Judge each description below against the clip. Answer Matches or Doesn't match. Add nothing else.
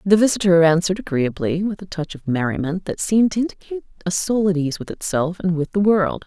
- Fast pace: Matches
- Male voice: Doesn't match